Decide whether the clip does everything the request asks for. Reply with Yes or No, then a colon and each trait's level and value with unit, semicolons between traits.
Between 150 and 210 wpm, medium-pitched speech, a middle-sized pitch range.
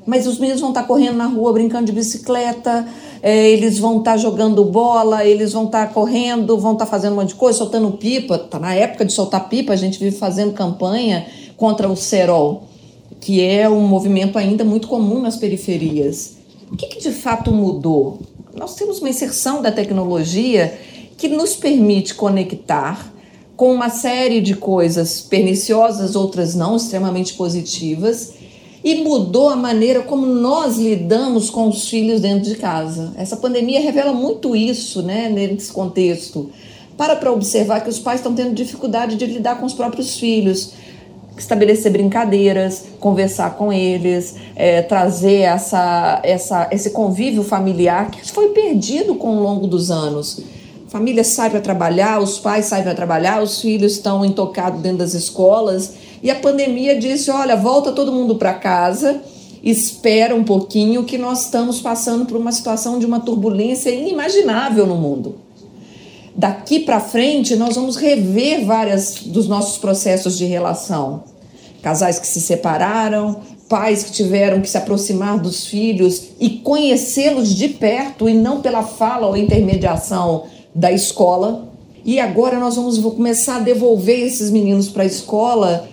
No: average, 155 wpm; high, 215 Hz; average, 3.8 semitones